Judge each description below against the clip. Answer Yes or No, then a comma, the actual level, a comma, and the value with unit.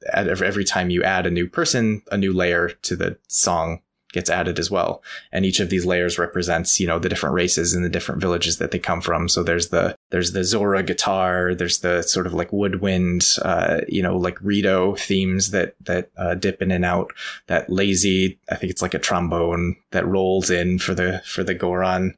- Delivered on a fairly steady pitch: Yes, narrow, 1.3 semitones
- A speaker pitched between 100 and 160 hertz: No, very low, 90 Hz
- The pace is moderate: No, fast, 210 wpm